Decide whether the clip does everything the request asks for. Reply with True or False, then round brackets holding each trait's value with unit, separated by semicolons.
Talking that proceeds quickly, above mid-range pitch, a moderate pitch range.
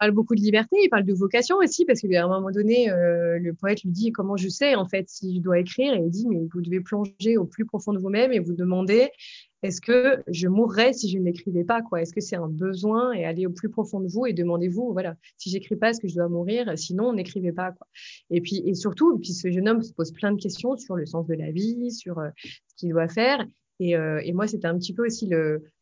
True (265 wpm; 195 Hz; 4.3 semitones)